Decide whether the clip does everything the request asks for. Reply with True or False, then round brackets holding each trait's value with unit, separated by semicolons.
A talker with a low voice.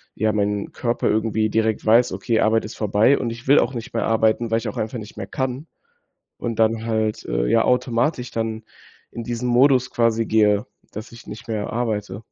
True (115 Hz)